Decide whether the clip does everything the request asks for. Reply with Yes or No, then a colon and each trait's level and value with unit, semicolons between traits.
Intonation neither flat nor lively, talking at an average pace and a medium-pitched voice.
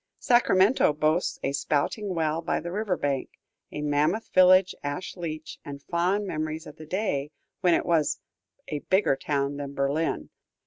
Yes: average, 4.3 semitones; average, 160 wpm; medium, 160 Hz